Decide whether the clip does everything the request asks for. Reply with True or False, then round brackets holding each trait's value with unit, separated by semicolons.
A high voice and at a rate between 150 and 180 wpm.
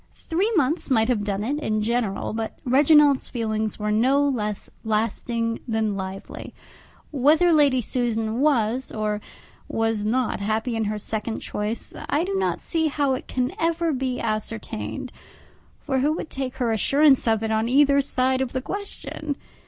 True (245 Hz; 160 wpm)